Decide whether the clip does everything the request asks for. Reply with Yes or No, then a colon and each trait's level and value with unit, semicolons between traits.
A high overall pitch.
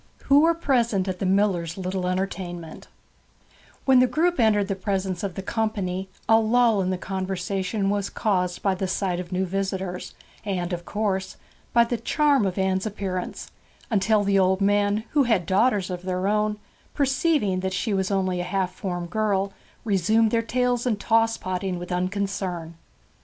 Yes: high, 195 Hz